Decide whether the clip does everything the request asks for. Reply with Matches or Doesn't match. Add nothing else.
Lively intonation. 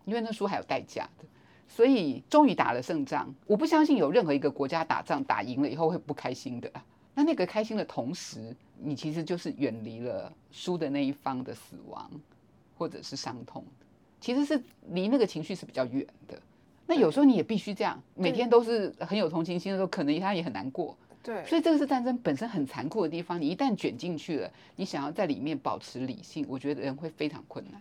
Matches